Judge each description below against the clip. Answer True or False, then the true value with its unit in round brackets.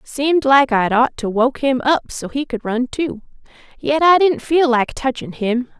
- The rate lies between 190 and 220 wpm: True (205 wpm)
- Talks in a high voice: True (260 Hz)